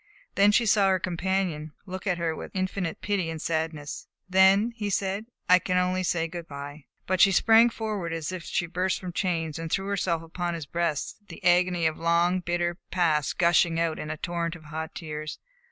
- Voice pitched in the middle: Yes, medium, 175 Hz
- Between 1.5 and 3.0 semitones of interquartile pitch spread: Yes, narrow, 2.5 semitones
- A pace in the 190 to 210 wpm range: Yes, average, 200 wpm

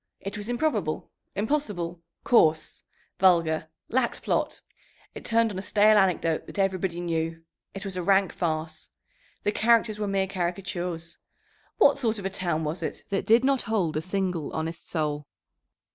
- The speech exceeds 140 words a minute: Yes, average, 160 wpm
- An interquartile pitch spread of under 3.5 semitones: No, average, 4.1 semitones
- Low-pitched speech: No, high, 190 Hz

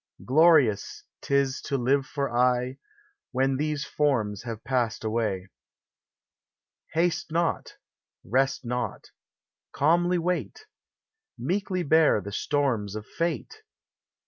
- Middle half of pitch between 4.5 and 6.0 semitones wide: Yes, wide, 5.5 semitones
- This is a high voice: No, low, 135 Hz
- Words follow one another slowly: Yes, slow, 110 wpm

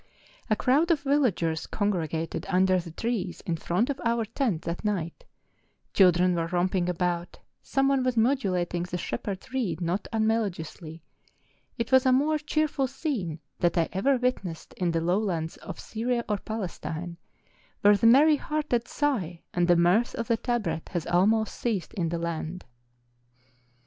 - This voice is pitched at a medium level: No, high, 195 Hz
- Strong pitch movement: Yes, wide, 5.9 semitones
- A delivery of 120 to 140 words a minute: No, average, 160 wpm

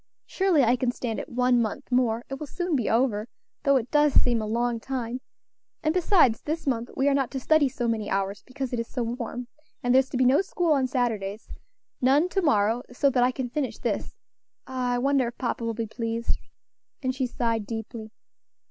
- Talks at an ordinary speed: No, fast, 210 wpm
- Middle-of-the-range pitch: No, very high, 250 Hz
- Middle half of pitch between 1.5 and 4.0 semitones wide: Yes, average, 2.8 semitones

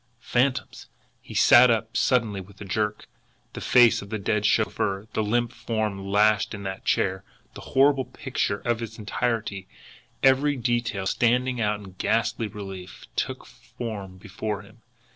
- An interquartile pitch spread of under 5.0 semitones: Yes, average, 3.1 semitones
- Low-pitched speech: Yes, low, 110 Hz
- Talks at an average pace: Yes, average, 150 wpm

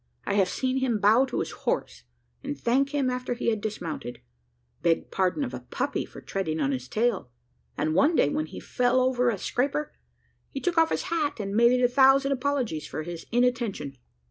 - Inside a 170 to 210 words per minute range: Yes, average, 200 wpm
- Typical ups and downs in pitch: No, wide, 6.4 semitones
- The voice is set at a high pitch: Yes, high, 240 Hz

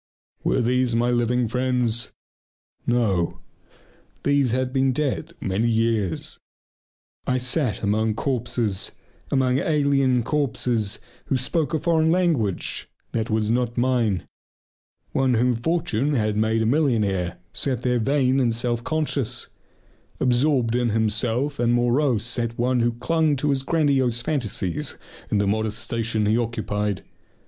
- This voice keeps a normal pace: No, slow, 130 wpm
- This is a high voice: No, low, 120 Hz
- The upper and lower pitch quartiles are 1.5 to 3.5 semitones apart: Yes, average, 3.2 semitones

